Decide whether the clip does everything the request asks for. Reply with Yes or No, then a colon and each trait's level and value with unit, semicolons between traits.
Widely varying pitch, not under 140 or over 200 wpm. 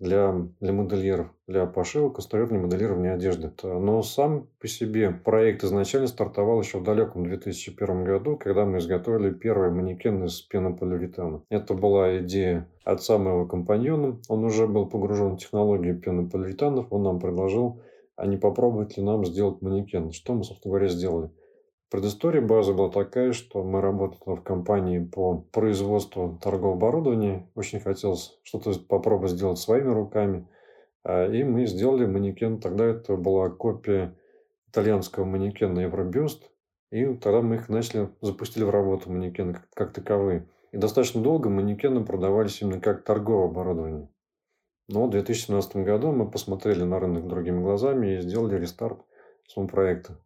No: average, 3.2 semitones; average, 145 wpm